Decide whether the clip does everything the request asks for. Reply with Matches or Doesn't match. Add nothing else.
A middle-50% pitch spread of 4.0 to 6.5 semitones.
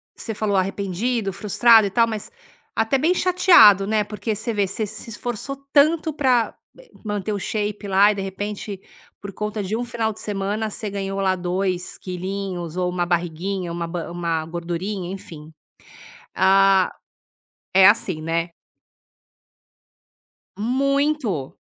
Doesn't match